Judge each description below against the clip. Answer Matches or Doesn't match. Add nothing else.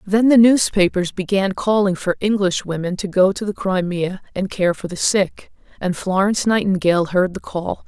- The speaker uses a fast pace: Doesn't match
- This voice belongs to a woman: Matches